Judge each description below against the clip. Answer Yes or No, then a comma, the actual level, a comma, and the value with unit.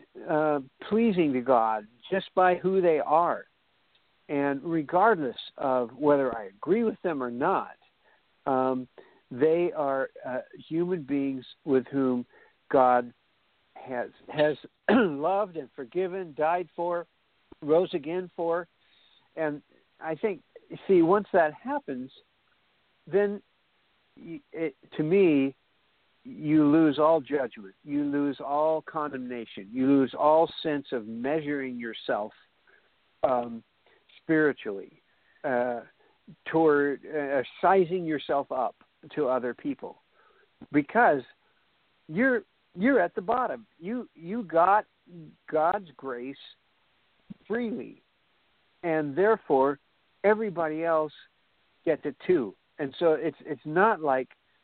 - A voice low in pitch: No, medium, 155 Hz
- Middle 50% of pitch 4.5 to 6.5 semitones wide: Yes, average, 5.2 semitones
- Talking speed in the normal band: No, slow, 110 wpm